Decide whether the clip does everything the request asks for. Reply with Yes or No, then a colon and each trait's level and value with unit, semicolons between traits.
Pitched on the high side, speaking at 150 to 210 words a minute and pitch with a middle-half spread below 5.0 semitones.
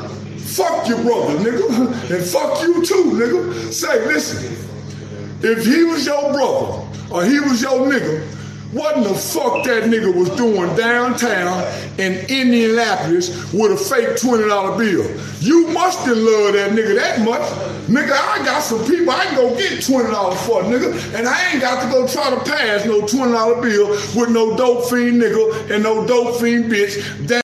Yes: high, 235 Hz; average, 175 wpm; average, 4.6 semitones